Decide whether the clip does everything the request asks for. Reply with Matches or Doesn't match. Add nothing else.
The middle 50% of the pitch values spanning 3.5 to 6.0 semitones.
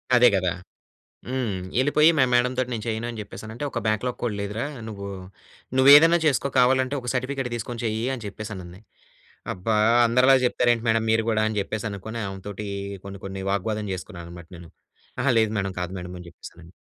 Matches